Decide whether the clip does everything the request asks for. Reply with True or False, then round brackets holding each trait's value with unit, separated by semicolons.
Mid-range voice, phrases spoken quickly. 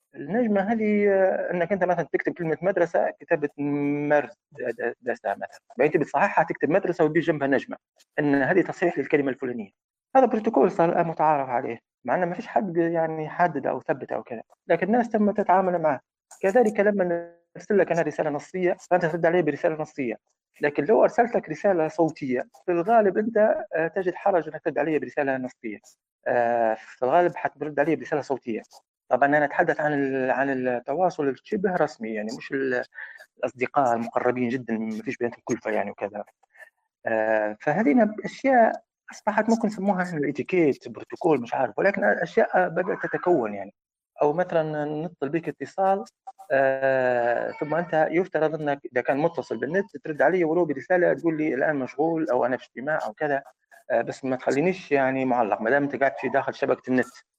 True (155 Hz; 160 wpm)